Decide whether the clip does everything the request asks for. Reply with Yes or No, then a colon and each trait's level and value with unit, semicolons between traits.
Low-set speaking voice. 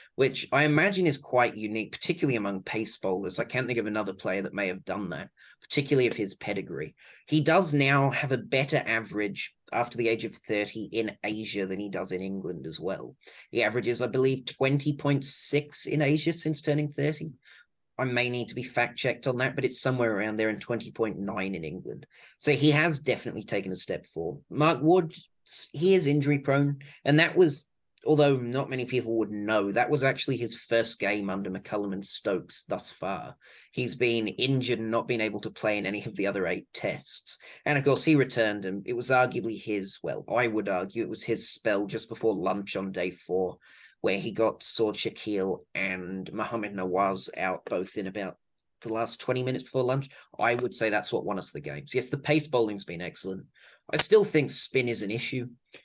Yes: low, 120 Hz